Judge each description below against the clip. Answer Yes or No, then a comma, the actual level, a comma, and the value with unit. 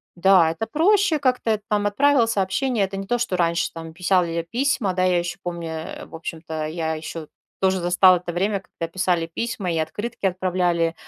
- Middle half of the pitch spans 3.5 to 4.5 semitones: Yes, average, 3.8 semitones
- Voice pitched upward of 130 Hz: Yes, medium, 185 Hz